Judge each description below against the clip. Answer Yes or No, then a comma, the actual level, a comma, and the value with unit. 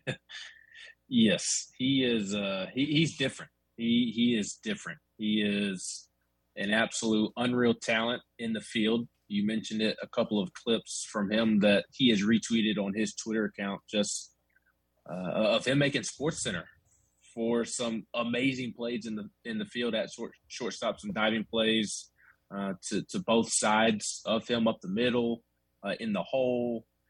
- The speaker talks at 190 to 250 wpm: No, average, 160 wpm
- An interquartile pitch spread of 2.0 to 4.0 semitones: Yes, average, 2.9 semitones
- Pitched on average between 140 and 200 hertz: No, low, 110 Hz